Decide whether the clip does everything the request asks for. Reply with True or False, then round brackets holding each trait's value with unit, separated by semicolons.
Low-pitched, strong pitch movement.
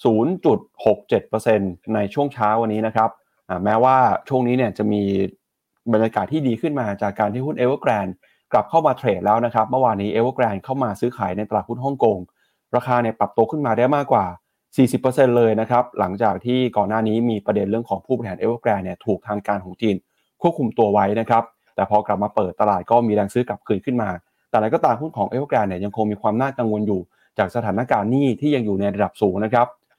False (110 Hz; 3.1 semitones)